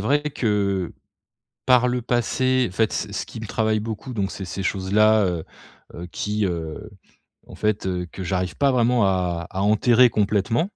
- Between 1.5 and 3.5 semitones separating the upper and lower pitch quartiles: No, average, 3.9 semitones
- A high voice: No, low, 105 Hz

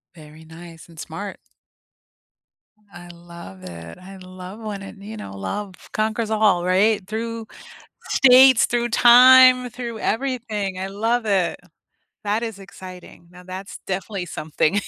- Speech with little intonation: No, average, 4.3 semitones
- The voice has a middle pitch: No, high, 195 Hz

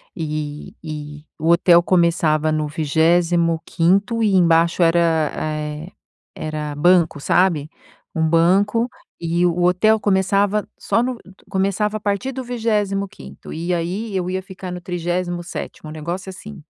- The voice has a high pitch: No, medium, 175 Hz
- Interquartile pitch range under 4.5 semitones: Yes, average, 3.4 semitones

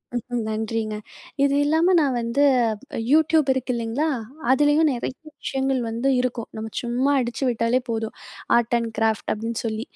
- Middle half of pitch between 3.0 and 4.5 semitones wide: Yes, average, 3.4 semitones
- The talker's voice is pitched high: Yes, high, 240 Hz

